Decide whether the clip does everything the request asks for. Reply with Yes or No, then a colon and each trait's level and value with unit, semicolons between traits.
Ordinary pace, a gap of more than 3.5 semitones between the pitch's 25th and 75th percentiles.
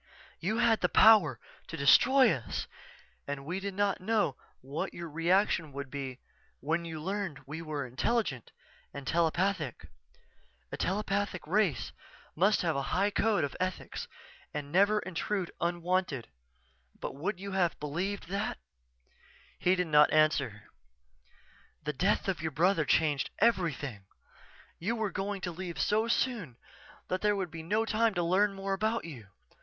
Yes: average, 150 wpm; average, 5.2 semitones